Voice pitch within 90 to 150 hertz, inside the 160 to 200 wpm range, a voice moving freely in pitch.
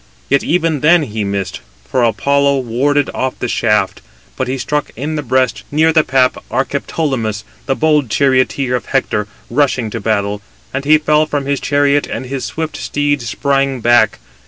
No: low, 135 Hz; average, 170 wpm; average, 3.2 semitones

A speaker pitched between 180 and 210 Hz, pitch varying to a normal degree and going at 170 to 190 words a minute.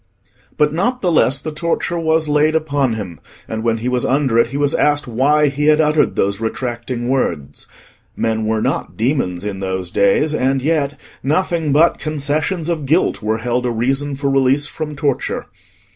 No: medium, 140 Hz; average, 4.6 semitones; average, 180 wpm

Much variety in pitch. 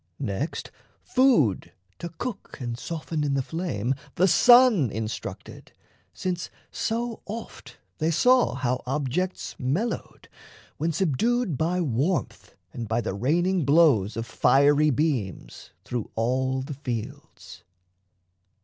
Yes: wide, 6.5 semitones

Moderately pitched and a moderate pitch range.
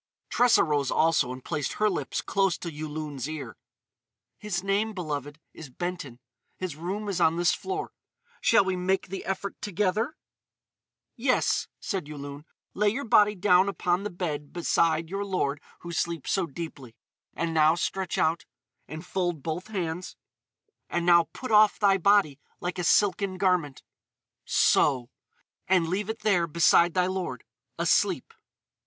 Yes: medium, 175 Hz; average, 4.1 semitones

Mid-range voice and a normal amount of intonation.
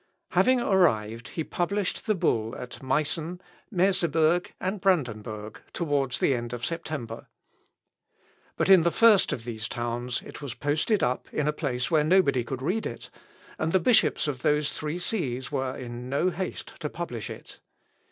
No: medium, 150 Hz; wide, 6.2 semitones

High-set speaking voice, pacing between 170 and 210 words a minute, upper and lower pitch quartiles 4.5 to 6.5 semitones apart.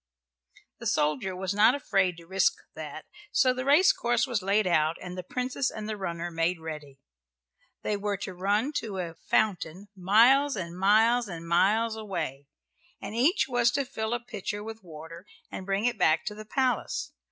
Yes: high, 200 Hz; average, 180 wpm; average, 5.0 semitones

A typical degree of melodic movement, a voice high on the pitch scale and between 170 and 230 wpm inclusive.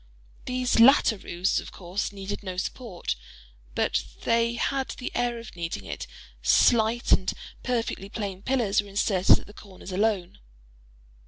No: average, 3.7 semitones; high, 210 Hz; average, 150 wpm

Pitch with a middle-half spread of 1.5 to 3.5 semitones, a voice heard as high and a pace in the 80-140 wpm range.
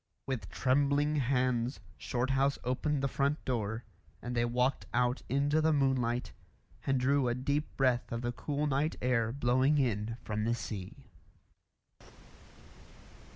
No: average, 2.7 semitones; low, 130 Hz; slow, 135 wpm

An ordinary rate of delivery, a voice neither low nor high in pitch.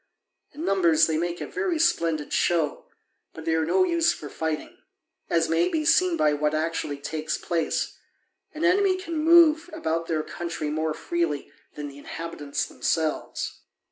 Yes: average, 160 wpm; medium, 165 Hz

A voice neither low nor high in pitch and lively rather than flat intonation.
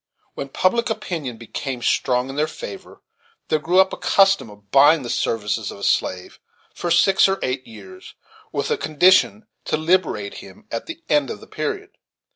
Yes: medium, 155 Hz; wide, 7.7 semitones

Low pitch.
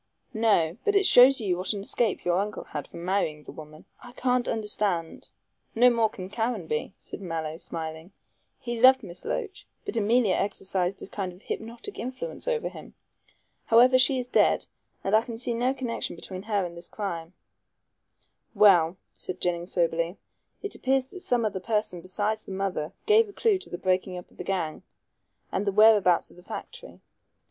No: high, 205 Hz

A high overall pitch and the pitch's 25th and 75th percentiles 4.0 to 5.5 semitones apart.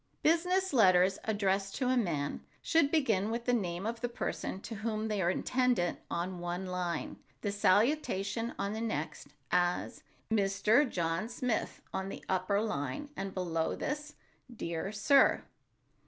Yes: high, 200 Hz; average, 4.7 semitones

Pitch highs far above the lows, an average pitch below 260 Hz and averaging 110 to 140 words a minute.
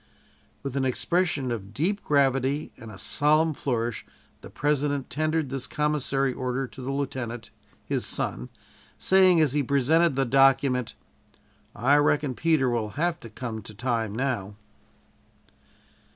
No: average, 3.5 semitones; low, 135 Hz; slow, 135 wpm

